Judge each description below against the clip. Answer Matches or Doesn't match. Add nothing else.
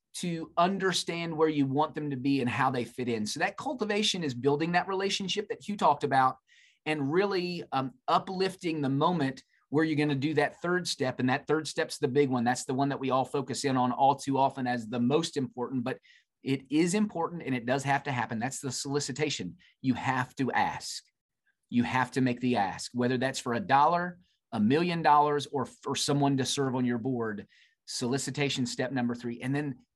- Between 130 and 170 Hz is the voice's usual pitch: Matches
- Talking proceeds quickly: Matches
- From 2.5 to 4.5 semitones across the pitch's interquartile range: Matches